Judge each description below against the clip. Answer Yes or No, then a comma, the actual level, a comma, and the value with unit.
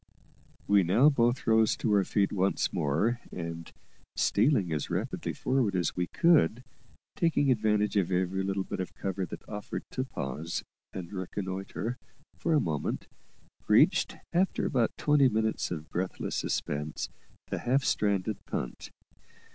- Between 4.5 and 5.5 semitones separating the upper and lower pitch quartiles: Yes, average, 5.1 semitones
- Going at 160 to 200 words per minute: No, average, 140 wpm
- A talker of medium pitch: No, low, 100 Hz